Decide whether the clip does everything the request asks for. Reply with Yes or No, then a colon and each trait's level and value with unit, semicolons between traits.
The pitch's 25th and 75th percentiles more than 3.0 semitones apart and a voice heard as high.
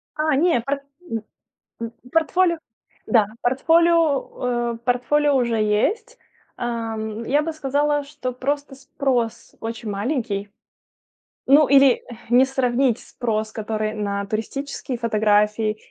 Yes: average, 4.4 semitones; very high, 250 Hz